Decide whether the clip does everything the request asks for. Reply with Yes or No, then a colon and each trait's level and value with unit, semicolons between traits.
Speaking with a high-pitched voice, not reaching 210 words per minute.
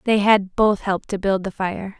No: high, 200 Hz; fast, 240 wpm